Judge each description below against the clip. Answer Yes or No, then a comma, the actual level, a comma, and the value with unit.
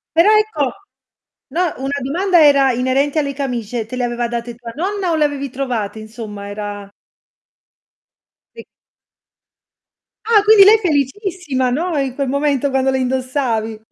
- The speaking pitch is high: Yes, very high, 270 Hz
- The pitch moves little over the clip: No, average, 5.0 semitones